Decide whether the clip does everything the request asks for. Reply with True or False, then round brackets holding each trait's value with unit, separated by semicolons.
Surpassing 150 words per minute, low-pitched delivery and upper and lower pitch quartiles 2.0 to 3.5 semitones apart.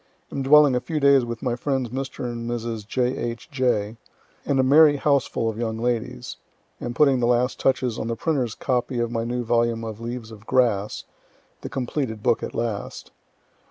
True (190 wpm; 120 Hz; 2.4 semitones)